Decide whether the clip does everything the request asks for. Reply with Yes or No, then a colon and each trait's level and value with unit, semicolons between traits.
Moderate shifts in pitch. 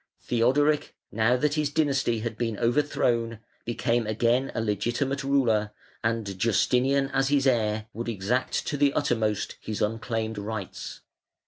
Yes: average, 3.7 semitones